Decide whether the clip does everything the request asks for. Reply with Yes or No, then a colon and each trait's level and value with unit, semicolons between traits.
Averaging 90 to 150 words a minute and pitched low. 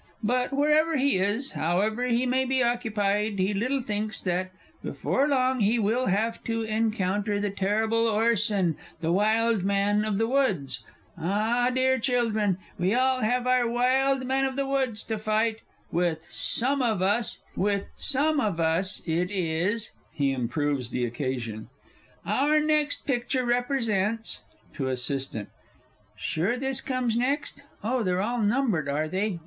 No: average, 140 wpm; high, 220 Hz